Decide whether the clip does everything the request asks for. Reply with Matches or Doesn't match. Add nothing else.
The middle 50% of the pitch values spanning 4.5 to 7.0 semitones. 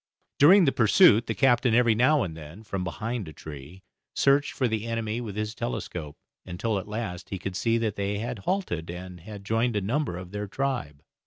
Matches